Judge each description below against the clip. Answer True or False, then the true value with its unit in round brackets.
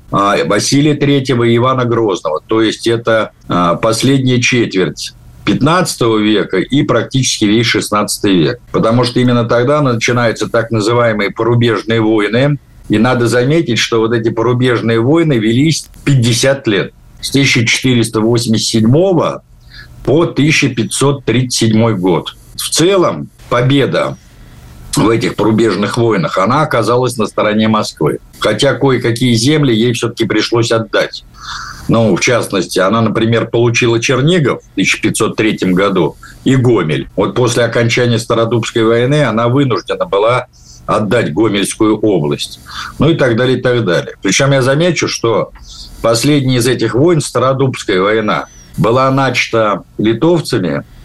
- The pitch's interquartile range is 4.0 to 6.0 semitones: False (2.8 semitones)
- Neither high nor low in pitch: False (120 Hz)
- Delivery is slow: False (120 wpm)